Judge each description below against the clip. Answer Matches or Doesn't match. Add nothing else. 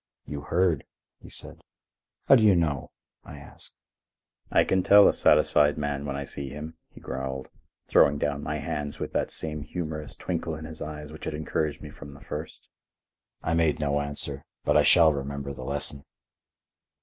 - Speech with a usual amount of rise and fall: Doesn't match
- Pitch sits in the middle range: Doesn't match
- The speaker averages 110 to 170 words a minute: Doesn't match